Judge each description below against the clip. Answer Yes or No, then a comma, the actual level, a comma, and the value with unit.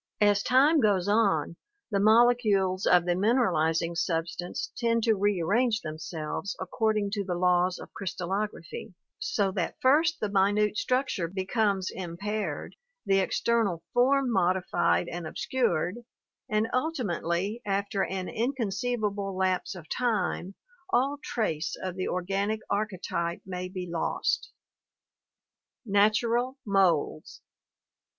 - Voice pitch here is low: No, high, 200 Hz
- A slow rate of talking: Yes, slow, 115 wpm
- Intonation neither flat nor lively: Yes, average, 3.8 semitones